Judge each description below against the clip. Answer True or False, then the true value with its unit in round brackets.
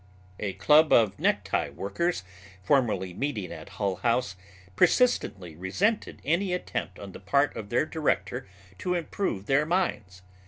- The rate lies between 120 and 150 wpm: True (140 wpm)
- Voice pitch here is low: True (115 Hz)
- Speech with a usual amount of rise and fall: False (8.6 semitones)